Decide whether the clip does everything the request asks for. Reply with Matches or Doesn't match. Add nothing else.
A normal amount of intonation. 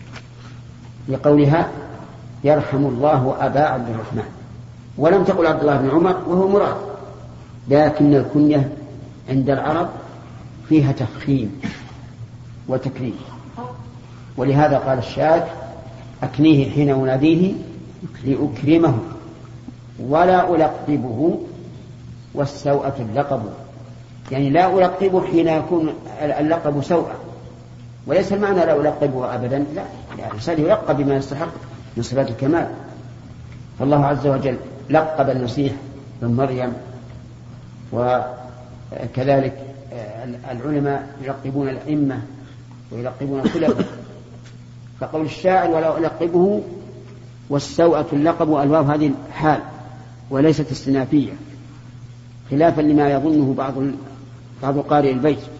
Matches